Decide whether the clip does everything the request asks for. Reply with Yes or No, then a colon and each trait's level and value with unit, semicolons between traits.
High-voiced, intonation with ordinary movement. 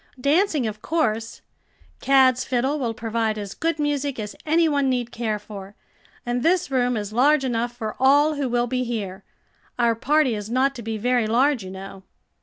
Yes: high, 245 Hz; average, 4.1 semitones